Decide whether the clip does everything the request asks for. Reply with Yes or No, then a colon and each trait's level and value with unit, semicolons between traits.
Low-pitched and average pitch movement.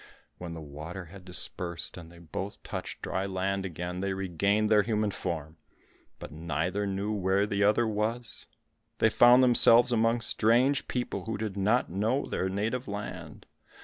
Yes: low, 100 Hz; average, 3.6 semitones